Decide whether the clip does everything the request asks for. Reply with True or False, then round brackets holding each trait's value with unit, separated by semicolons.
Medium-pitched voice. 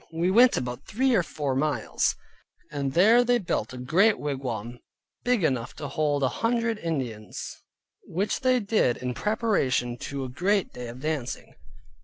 True (155 Hz)